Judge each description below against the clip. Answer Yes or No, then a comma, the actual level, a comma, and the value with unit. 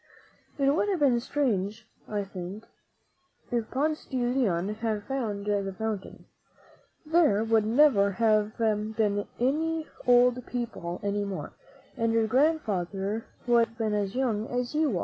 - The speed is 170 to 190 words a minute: No, average, 150 wpm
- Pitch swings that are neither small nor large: Yes, average, 3.7 semitones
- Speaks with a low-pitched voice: No, high, 225 Hz